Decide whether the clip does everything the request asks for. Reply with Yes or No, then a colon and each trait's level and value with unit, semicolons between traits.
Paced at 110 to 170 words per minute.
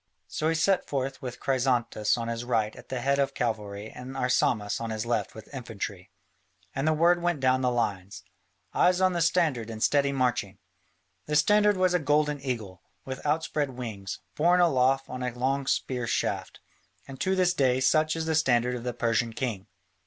No: average, 190 wpm